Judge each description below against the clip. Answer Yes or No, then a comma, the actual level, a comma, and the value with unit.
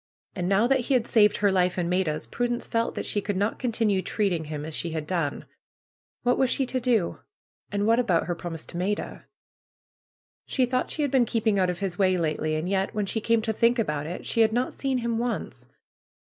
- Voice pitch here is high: Yes, high, 205 Hz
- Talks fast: Yes, fast, 225 wpm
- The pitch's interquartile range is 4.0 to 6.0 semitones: Yes, average, 5.0 semitones